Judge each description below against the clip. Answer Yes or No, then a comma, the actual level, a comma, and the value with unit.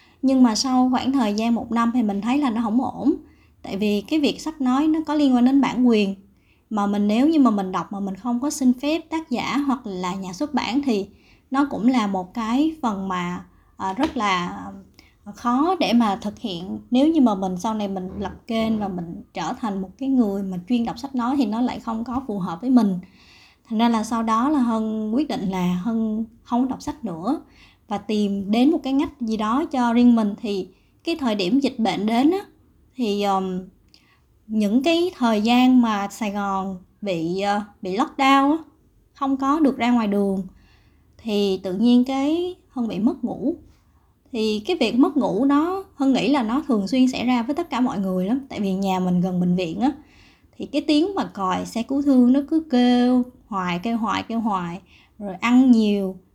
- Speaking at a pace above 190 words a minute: Yes, average, 210 wpm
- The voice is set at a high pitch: Yes, high, 235 Hz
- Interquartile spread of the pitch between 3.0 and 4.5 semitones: No, average, 5.0 semitones